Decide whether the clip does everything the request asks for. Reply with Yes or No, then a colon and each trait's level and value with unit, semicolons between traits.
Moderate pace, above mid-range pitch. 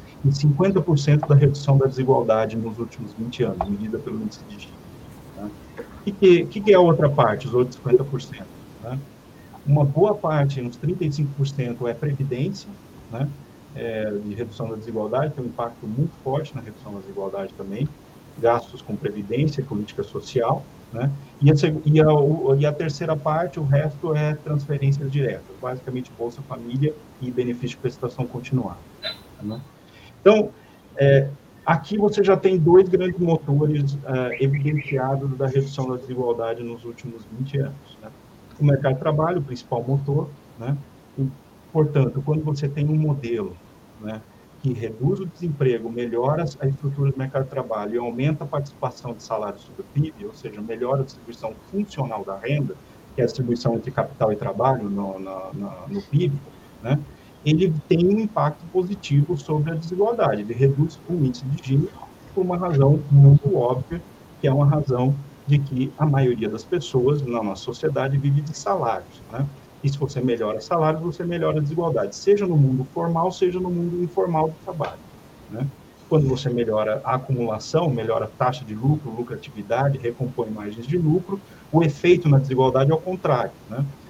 No: average, 165 wpm; medium, 140 Hz